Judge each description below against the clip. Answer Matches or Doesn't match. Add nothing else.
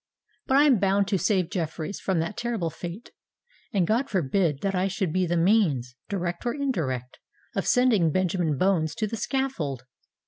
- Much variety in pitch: Doesn't match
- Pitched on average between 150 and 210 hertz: Matches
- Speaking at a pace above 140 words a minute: Matches